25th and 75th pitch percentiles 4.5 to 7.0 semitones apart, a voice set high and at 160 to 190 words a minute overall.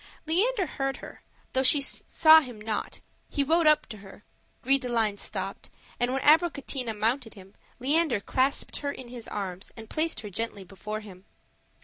Yes: average, 5.2 semitones; very high, 250 Hz; average, 170 wpm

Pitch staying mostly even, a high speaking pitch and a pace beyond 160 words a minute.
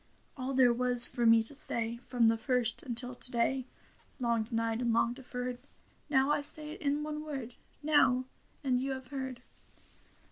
Yes: narrow, 2.2 semitones; very high, 250 Hz; average, 180 wpm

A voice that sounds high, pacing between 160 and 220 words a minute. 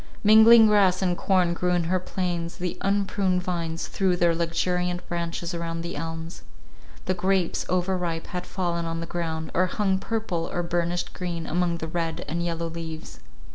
No: medium, 175 Hz; average, 170 wpm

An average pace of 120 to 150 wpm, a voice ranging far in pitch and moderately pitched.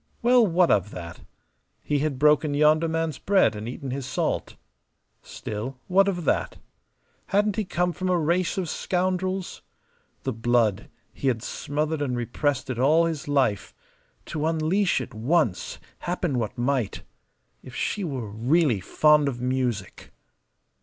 Yes: average, 145 wpm; wide, 5.8 semitones; medium, 145 Hz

